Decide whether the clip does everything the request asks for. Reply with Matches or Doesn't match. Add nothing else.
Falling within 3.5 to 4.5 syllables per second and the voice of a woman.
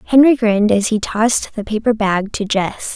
Doesn't match